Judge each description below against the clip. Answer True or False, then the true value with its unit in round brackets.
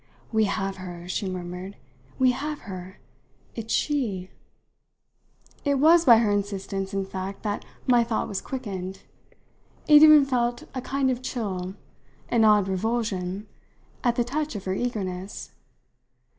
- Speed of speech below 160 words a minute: True (140 wpm)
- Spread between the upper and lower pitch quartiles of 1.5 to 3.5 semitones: False (4.8 semitones)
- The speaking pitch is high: True (210 Hz)